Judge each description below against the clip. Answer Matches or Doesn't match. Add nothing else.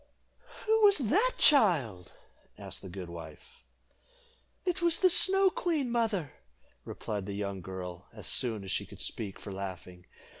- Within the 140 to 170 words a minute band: Matches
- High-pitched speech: Doesn't match